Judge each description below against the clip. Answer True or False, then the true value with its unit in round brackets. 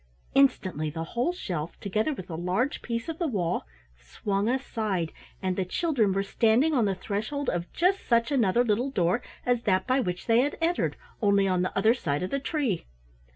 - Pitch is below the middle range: False (215 Hz)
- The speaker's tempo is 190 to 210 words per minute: True (195 wpm)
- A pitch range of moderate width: False (6.1 semitones)